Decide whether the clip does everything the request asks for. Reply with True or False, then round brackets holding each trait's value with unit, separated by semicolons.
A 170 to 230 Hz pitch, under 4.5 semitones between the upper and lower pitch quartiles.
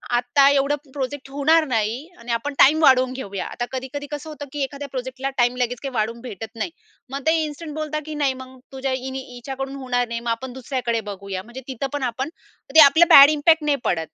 False (265 Hz; 2.9 semitones)